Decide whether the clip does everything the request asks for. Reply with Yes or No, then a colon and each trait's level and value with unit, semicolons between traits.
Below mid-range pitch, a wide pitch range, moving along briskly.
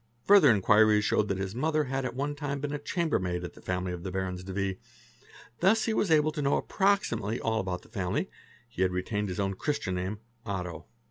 Yes: low, 105 Hz; wide, 7.8 semitones; fast, 220 wpm